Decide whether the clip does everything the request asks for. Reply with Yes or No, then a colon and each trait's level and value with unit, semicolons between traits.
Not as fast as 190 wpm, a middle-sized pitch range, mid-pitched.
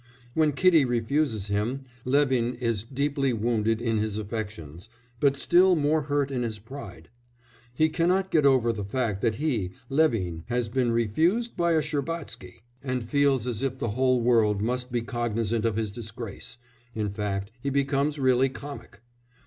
No: average, 160 wpm; average, 4.3 semitones; low, 125 Hz